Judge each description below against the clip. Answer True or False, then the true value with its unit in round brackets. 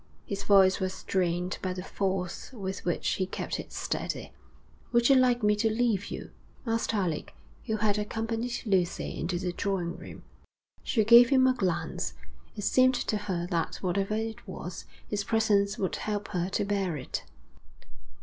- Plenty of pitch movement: False (3.3 semitones)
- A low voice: False (200 Hz)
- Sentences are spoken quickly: False (170 wpm)